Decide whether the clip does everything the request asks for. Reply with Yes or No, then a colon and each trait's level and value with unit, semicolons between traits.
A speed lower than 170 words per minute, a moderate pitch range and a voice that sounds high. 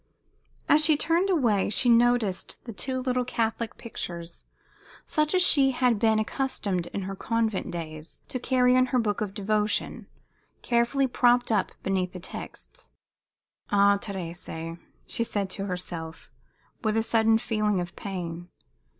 Yes: average, 140 wpm; average, 4.7 semitones; high, 220 Hz